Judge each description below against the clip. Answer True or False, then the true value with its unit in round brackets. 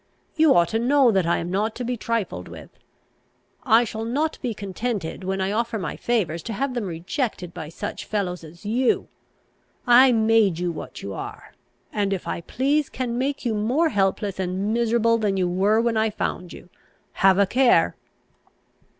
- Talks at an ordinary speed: True (185 wpm)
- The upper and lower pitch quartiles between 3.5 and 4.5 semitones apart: True (4.2 semitones)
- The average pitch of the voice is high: True (215 Hz)